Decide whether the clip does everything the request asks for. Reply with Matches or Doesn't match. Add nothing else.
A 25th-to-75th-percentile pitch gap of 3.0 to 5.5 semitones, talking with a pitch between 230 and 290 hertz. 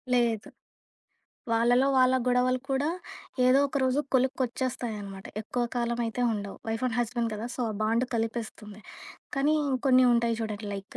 Doesn't match